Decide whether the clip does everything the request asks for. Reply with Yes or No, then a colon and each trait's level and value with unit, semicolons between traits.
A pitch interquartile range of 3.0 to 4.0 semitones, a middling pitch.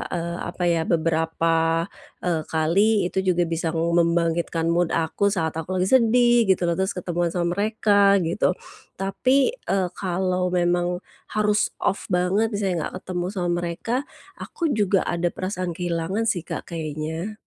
No: narrow, 2.5 semitones; medium, 175 Hz